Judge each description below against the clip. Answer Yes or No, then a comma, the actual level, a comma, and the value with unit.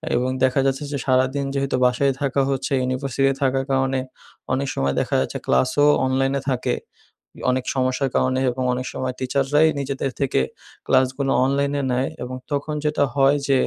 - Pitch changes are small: Yes, narrow, 1.2 semitones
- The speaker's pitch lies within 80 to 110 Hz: No, low, 135 Hz